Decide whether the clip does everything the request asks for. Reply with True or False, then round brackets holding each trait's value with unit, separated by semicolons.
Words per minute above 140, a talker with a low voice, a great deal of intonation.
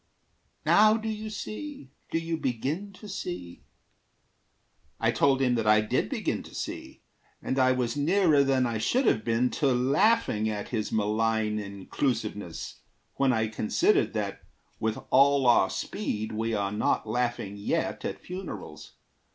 True (150 wpm; 125 Hz; 6.1 semitones)